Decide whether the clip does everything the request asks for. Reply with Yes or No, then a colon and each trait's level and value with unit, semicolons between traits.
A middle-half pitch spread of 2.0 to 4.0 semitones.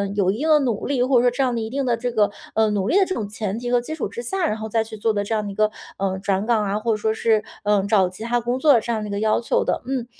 Yes: average, 2.8 semitones